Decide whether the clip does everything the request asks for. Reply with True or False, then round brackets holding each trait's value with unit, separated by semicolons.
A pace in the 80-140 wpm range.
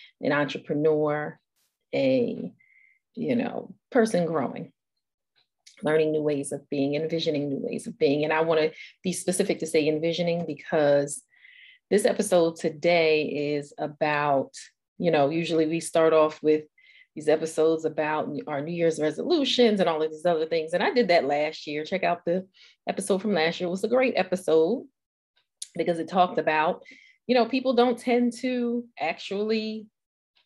False (160 wpm)